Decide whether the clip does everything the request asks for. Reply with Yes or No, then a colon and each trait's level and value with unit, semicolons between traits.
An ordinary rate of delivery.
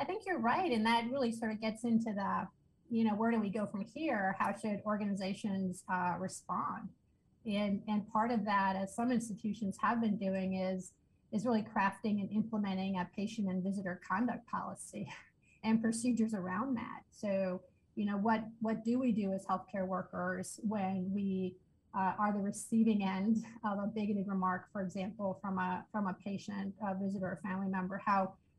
Yes: average, 185 wpm